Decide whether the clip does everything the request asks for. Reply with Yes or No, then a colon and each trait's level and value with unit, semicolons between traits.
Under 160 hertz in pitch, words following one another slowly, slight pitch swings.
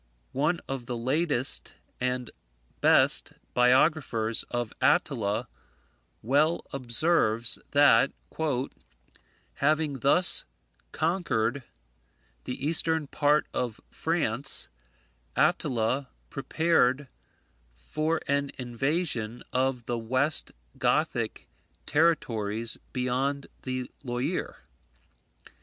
No: low, 135 Hz; slow, 75 wpm; average, 4.0 semitones